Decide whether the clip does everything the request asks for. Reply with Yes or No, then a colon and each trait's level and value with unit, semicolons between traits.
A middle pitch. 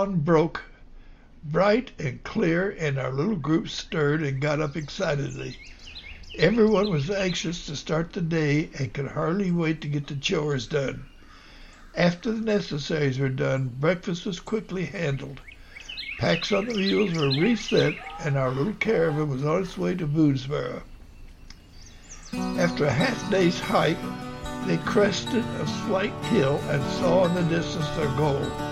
Yes: medium, 155 Hz